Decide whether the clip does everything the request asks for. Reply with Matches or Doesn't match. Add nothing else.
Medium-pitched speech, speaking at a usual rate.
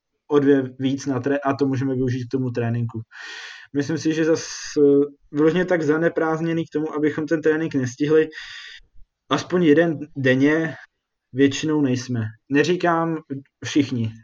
Matches